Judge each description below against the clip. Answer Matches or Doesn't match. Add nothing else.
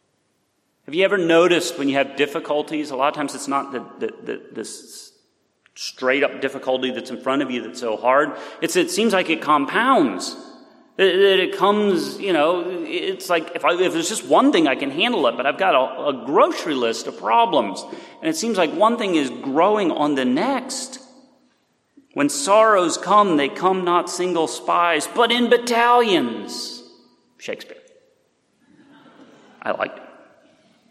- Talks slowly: Doesn't match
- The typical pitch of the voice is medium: Doesn't match